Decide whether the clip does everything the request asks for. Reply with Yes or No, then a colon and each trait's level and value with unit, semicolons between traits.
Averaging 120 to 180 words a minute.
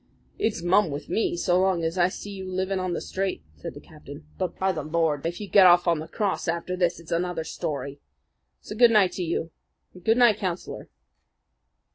No: average, 195 wpm